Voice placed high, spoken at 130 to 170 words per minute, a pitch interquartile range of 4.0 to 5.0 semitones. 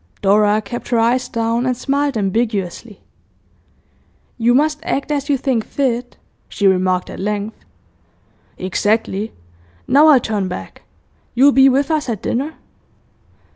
Yes: high, 235 Hz; slow, 135 wpm; average, 4.6 semitones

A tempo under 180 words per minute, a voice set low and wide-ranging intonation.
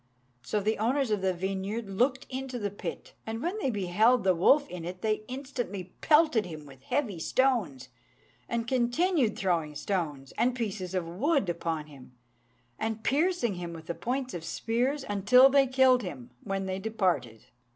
No: average, 170 wpm; high, 215 Hz; wide, 6.3 semitones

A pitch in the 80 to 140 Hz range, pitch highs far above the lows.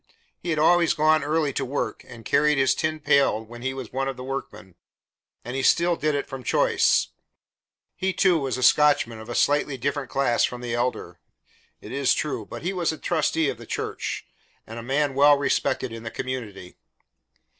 No: low, 135 Hz; average, 3.5 semitones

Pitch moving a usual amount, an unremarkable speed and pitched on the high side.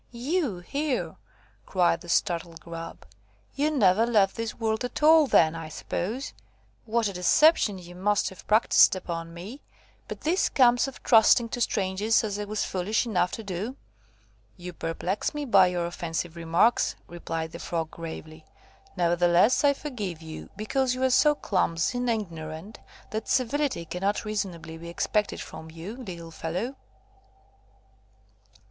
No: wide, 5.9 semitones; average, 150 wpm; high, 195 Hz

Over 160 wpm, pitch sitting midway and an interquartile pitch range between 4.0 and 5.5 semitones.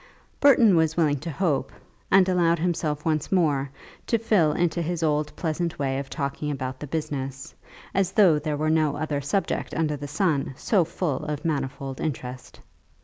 No: average, 170 wpm; medium, 155 Hz; average, 3.3 semitones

